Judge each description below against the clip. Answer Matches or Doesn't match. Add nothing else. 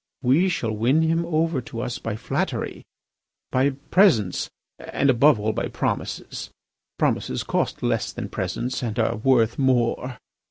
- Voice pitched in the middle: Doesn't match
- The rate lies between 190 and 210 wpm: Doesn't match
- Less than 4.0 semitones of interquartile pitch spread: Doesn't match